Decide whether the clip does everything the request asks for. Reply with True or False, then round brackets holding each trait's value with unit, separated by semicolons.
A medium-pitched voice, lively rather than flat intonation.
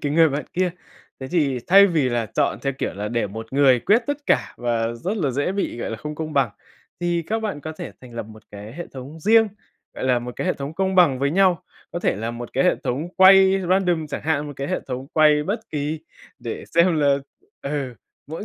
True (150 Hz; 5.9 semitones)